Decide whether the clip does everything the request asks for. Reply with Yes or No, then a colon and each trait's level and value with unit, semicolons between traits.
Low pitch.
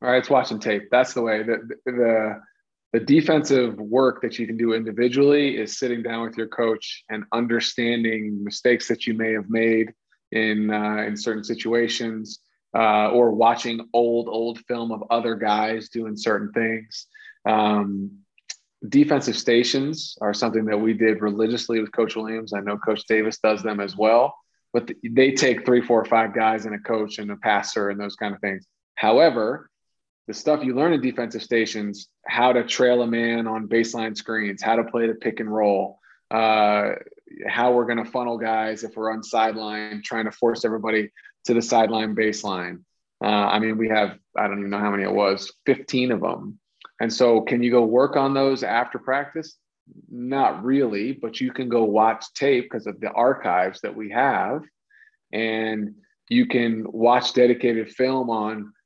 Yes: low, 115 Hz